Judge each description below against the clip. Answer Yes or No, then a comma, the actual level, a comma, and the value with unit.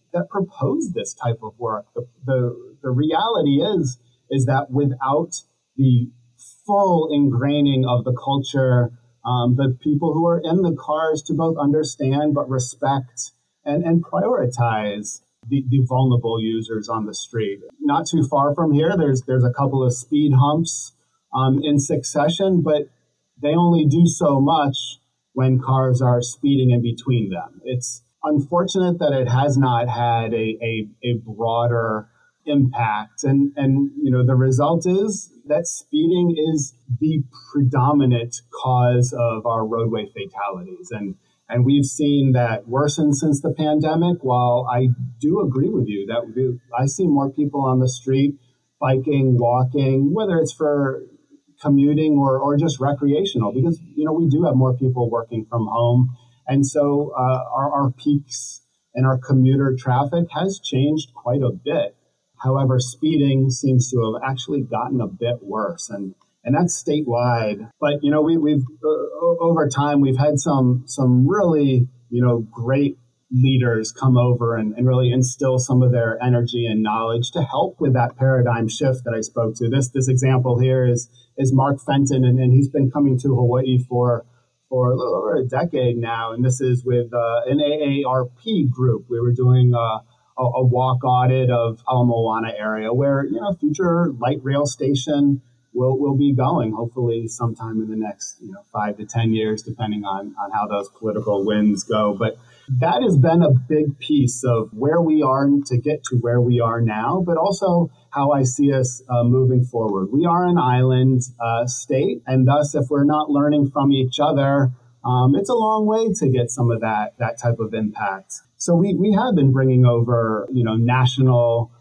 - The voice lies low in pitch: Yes, low, 130 Hz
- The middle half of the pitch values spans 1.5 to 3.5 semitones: Yes, average, 3.2 semitones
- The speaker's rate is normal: Yes, average, 175 wpm